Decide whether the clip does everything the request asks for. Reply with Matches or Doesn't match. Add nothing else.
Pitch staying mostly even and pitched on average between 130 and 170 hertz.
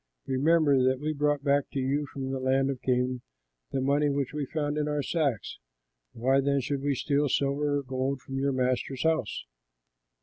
Matches